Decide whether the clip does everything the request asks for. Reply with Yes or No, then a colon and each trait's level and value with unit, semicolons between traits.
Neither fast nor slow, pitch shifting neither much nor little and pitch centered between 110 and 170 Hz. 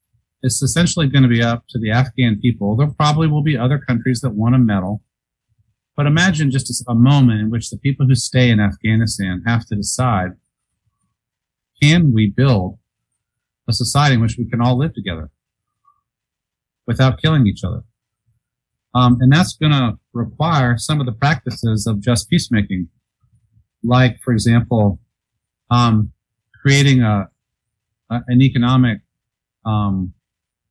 Yes: average, 145 wpm; average, 3.1 semitones; low, 120 Hz